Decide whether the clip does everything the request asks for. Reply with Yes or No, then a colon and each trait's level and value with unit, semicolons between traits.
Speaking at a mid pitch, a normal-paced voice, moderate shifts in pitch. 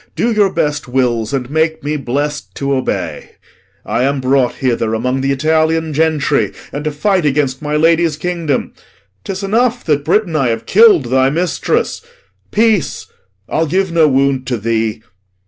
Yes: medium, 150 Hz; average, 160 wpm; average, 4.0 semitones